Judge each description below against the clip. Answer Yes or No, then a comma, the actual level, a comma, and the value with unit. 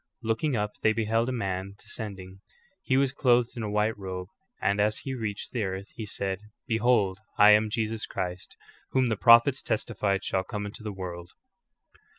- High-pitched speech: No, low, 105 Hz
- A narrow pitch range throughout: No, average, 3.1 semitones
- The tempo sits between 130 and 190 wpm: Yes, average, 185 wpm